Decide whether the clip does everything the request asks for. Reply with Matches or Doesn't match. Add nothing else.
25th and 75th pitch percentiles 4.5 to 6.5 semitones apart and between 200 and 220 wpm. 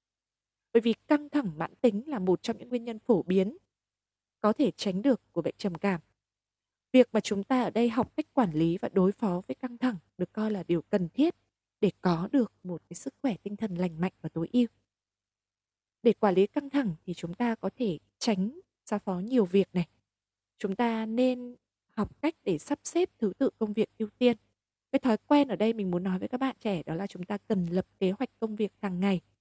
Doesn't match